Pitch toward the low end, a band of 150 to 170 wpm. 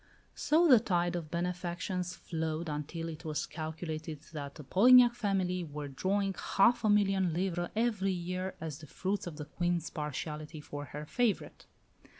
No: medium, 175 Hz; average, 155 wpm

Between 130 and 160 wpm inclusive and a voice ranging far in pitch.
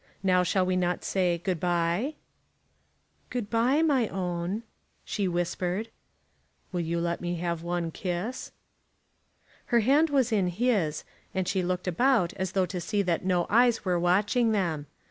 No: average, 155 wpm; average, 4.1 semitones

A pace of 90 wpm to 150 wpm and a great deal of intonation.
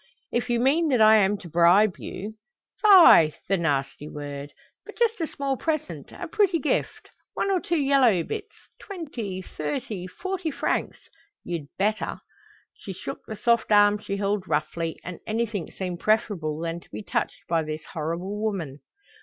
No: average, 165 wpm; wide, 8.1 semitones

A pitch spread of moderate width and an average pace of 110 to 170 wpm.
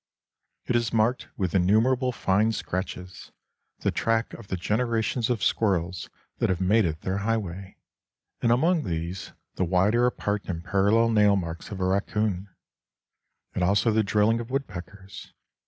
Yes: average, 3.5 semitones; average, 150 wpm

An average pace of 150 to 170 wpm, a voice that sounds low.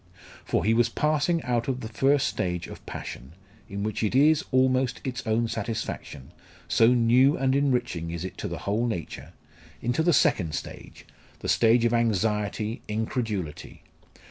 Yes: average, 160 wpm; low, 115 Hz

